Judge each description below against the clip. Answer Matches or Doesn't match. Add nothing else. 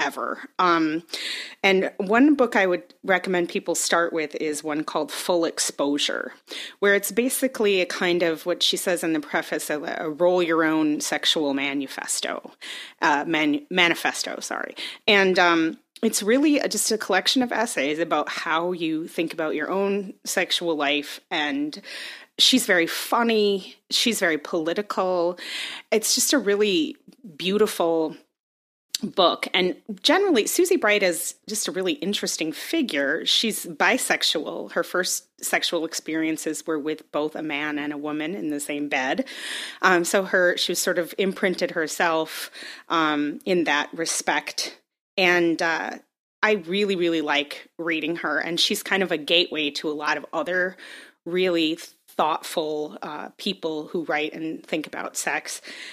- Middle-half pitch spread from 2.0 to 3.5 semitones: Doesn't match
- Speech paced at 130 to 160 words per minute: Matches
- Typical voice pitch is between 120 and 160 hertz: Doesn't match